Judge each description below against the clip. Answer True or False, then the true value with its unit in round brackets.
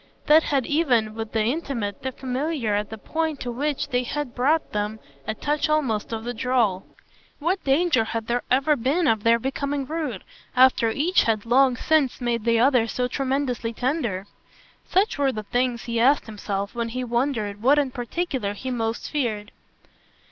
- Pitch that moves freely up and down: False (4.0 semitones)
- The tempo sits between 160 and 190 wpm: True (175 wpm)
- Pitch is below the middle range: False (250 Hz)